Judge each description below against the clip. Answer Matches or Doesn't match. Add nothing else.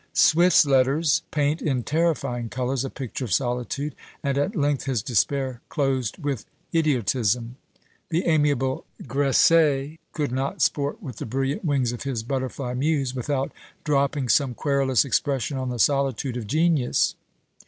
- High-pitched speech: Doesn't match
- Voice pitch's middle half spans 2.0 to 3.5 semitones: Matches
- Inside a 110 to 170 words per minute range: Matches